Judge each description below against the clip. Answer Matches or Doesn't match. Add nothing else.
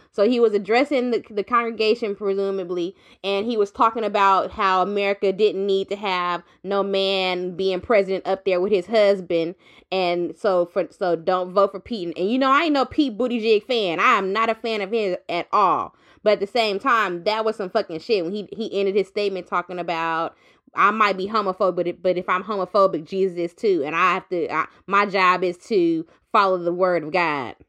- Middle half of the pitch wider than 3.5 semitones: Doesn't match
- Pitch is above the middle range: Matches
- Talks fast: Matches